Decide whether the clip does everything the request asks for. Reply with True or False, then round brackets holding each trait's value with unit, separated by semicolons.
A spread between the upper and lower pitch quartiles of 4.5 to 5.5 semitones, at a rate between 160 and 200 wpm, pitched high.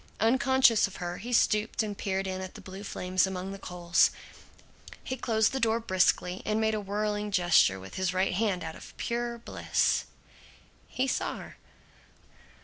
False (3.3 semitones; 170 wpm; 200 Hz)